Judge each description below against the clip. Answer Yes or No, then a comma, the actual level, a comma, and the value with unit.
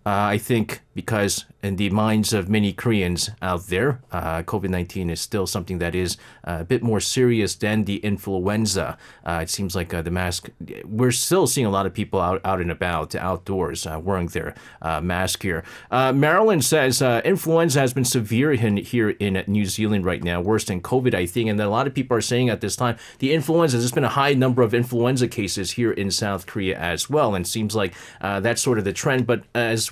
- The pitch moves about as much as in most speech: Yes, average, 4.6 semitones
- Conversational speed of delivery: No, fast, 220 wpm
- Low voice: Yes, low, 105 Hz